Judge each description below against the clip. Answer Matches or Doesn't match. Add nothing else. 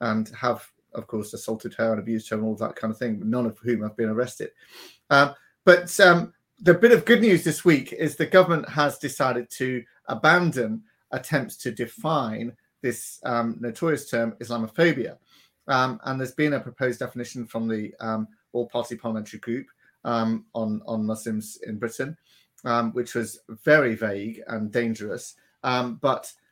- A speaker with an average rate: Matches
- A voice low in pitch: Matches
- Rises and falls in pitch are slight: Doesn't match